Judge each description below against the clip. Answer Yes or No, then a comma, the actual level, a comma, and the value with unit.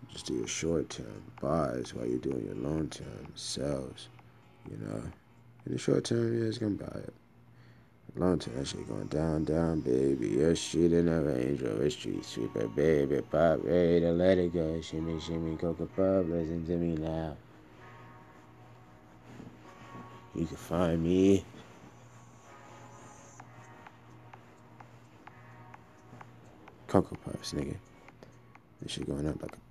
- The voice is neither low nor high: No, very low, 80 Hz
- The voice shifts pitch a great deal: Yes, wide, 5.7 semitones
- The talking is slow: No, average, 145 wpm